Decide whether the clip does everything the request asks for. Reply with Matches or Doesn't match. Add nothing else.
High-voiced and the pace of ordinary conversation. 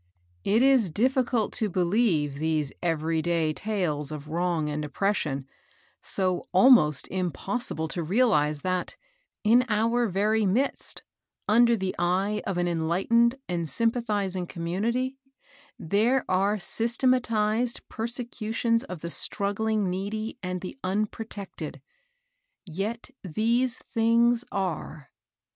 Doesn't match